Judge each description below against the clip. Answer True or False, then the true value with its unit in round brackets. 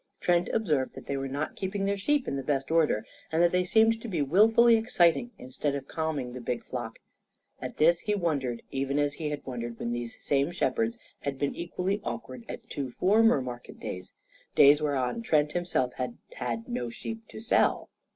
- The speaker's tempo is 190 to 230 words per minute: True (195 wpm)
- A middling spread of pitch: False (6.8 semitones)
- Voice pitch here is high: False (150 Hz)